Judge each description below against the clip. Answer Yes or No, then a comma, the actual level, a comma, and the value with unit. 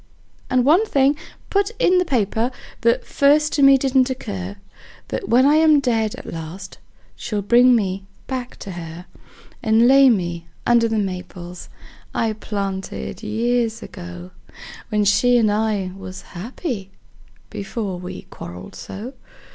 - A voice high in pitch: Yes, high, 220 Hz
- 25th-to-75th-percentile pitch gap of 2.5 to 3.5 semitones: No, average, 5.1 semitones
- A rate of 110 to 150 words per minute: Yes, average, 140 wpm